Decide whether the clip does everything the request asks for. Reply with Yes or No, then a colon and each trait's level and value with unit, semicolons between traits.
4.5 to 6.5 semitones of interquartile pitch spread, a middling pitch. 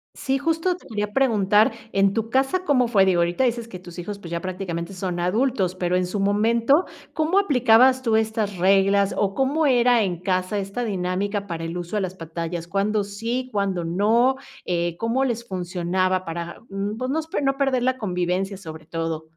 No: average, 5.1 semitones; high, 200 Hz